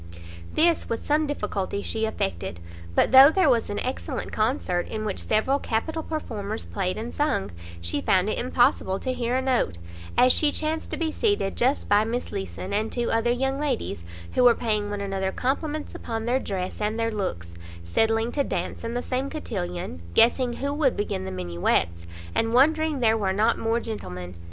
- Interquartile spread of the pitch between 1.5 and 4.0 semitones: No, average, 5.3 semitones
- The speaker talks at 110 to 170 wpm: No, average, 185 wpm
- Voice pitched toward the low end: No, high, 225 Hz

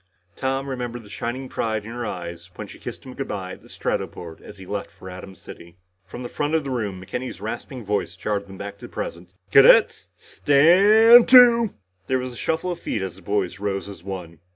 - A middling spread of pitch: No, wide, 5.9 semitones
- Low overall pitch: Yes, low, 110 Hz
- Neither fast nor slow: No, fast, 220 wpm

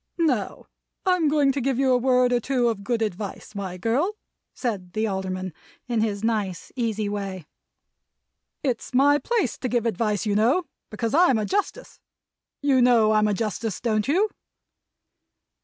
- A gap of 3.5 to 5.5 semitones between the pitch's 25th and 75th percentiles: Yes, average, 4.3 semitones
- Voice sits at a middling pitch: No, high, 230 Hz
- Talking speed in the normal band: Yes, average, 160 wpm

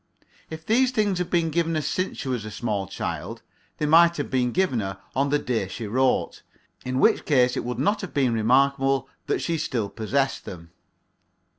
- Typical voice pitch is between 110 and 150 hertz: Yes, low, 135 Hz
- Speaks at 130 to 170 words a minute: No, average, 190 wpm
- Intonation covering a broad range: Yes, wide, 5.7 semitones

